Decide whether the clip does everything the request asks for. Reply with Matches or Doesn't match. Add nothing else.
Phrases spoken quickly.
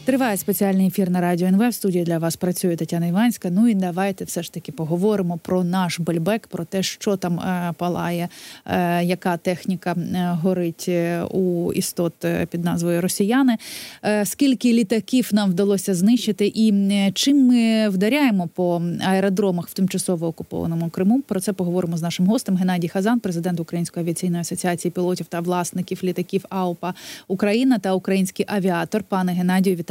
Matches